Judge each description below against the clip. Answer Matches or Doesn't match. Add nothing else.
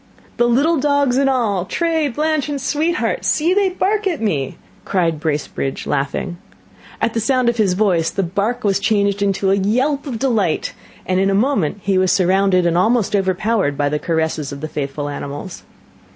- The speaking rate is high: Doesn't match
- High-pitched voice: Matches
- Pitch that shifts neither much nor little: Doesn't match